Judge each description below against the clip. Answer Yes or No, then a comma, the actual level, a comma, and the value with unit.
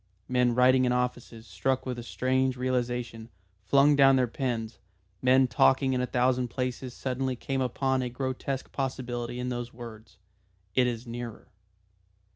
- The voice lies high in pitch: No, low, 125 Hz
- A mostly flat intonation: Yes, narrow, 1.4 semitones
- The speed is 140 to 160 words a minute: Yes, average, 150 wpm